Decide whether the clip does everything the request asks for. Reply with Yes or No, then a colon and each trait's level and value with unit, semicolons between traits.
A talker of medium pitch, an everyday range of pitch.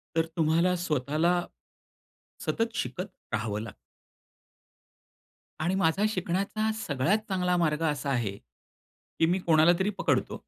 Yes: medium, 170 Hz; average, 3.5 semitones